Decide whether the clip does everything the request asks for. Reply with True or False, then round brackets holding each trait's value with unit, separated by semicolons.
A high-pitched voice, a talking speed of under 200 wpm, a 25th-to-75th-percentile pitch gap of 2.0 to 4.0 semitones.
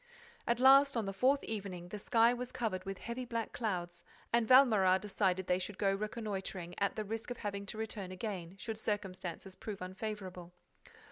True (205 Hz; 185 wpm; 3.4 semitones)